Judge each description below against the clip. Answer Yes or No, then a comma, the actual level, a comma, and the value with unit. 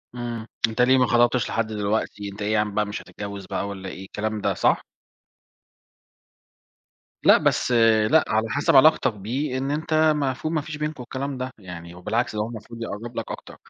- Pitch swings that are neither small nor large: Yes, average, 4.1 semitones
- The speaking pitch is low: Yes, low, 115 Hz